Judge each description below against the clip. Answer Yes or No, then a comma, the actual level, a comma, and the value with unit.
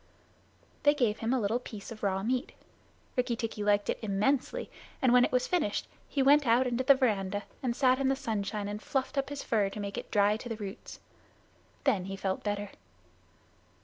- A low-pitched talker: No, high, 225 Hz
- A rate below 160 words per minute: No, average, 200 wpm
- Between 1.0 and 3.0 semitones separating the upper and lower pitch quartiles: No, average, 4.2 semitones